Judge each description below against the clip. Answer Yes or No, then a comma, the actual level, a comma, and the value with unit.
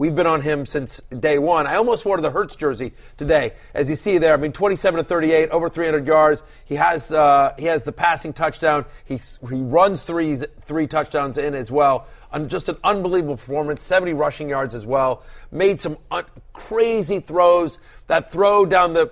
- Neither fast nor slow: Yes, average, 195 wpm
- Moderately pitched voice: Yes, medium, 155 Hz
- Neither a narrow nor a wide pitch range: Yes, average, 3.2 semitones